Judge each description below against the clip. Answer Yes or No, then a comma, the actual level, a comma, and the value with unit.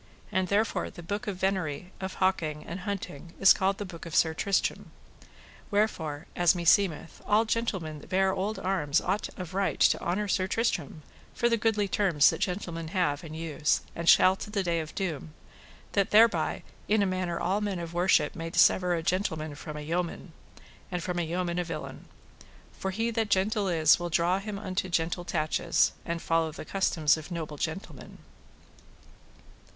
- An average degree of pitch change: Yes, average, 3.1 semitones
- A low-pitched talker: No, medium, 180 Hz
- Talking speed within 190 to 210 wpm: No, average, 180 wpm